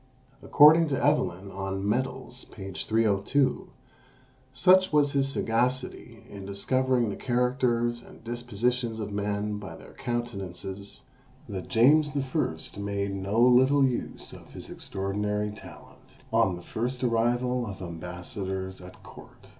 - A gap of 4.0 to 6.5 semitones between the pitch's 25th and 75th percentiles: Yes, average, 4.5 semitones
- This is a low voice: Yes, low, 115 Hz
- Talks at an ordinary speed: No, slow, 125 wpm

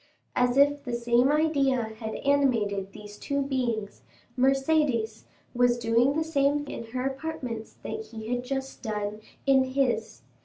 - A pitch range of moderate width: Yes, average, 3.6 semitones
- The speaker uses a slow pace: No, average, 145 wpm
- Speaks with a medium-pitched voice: No, very high, 250 Hz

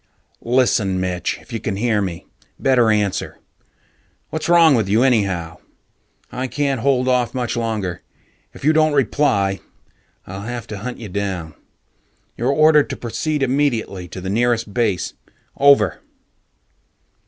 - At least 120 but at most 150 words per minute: Yes, average, 140 wpm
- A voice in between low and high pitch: No, low, 115 Hz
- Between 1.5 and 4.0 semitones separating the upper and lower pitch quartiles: No, average, 5.3 semitones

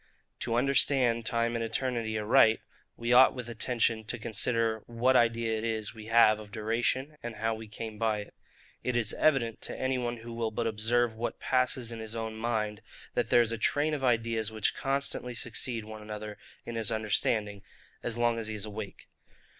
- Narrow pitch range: Yes, narrow, 1.5 semitones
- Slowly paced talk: No, average, 195 wpm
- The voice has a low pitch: Yes, low, 115 Hz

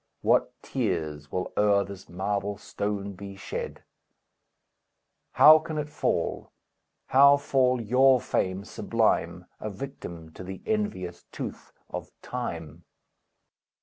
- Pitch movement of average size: No, wide, 6.1 semitones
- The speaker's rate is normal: No, slow, 115 wpm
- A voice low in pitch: Yes, low, 100 Hz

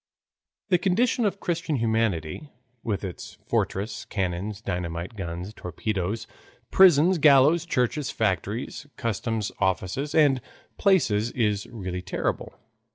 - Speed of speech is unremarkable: No, slow, 105 wpm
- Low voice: Yes, low, 110 Hz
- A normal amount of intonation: No, wide, 7.8 semitones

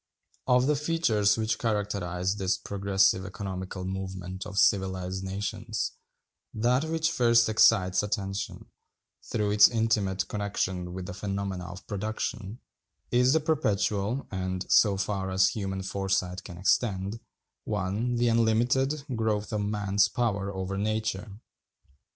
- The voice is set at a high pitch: No, low, 100 Hz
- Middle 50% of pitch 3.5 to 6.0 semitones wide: No, average, 2.8 semitones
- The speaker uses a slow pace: Yes, slow, 125 wpm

